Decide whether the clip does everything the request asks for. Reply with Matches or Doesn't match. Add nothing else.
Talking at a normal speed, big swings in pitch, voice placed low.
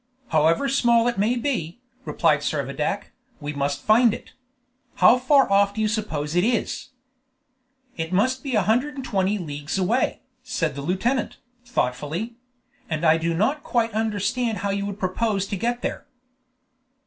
Doesn't match